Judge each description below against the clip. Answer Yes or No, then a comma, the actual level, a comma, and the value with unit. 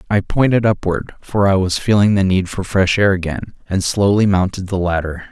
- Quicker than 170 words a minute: Yes, fast, 205 wpm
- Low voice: Yes, very low, 95 Hz